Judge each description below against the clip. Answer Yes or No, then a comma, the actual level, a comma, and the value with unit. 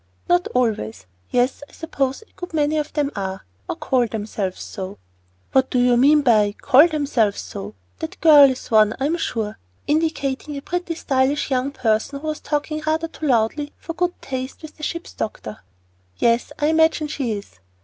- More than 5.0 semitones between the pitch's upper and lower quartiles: Yes, wide, 5.5 semitones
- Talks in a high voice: Yes, very high, 270 Hz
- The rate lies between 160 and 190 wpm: Yes, average, 180 wpm